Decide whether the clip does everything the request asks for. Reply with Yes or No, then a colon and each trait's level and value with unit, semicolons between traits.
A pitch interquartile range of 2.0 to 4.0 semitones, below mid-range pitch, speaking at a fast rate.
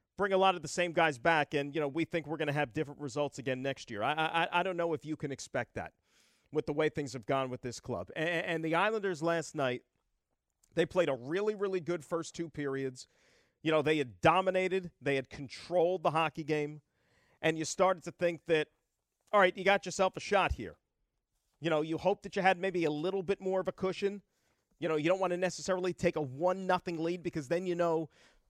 No: average, 3.5 semitones; medium, 165 Hz; fast, 235 wpm